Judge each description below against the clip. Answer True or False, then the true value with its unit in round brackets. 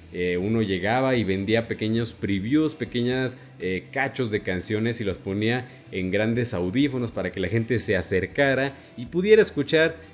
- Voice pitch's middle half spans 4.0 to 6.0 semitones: True (4.7 semitones)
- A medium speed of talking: True (160 wpm)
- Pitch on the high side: False (115 Hz)